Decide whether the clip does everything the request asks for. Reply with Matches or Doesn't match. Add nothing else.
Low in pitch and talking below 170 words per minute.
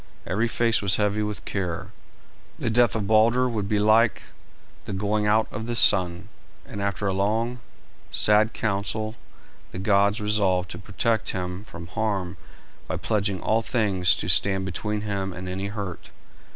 Matches